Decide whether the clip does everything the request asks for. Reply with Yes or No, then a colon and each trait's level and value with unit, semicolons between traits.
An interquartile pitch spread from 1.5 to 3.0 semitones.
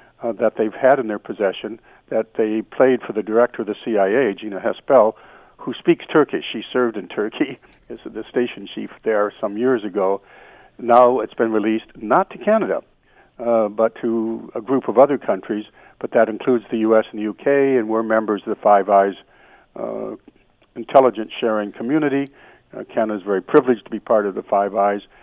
Yes: narrow, 2.6 semitones